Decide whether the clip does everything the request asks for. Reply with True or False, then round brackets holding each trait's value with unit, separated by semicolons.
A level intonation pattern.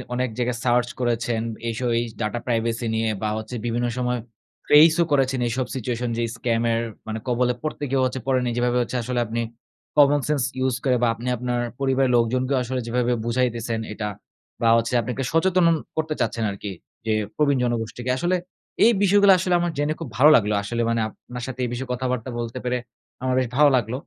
True (2.2 semitones)